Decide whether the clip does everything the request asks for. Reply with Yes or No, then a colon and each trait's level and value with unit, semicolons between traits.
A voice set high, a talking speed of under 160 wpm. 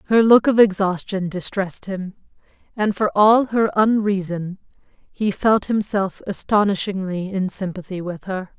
Yes: high, 195 Hz; slow, 135 wpm